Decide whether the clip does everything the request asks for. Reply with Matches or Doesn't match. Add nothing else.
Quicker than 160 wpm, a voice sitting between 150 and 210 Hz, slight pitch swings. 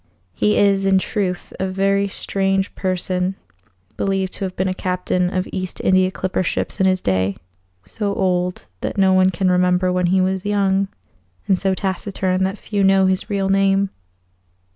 Matches